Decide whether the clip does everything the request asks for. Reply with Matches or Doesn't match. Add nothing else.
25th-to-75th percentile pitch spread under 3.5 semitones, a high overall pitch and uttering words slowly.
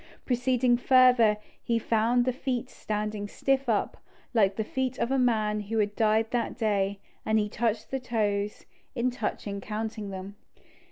Doesn't match